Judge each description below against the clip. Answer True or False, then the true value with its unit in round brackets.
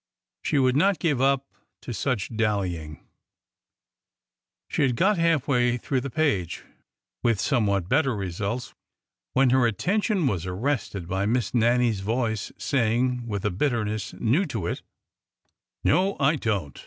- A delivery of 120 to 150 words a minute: True (140 wpm)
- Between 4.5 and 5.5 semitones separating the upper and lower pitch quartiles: True (5.2 semitones)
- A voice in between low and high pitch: False (120 Hz)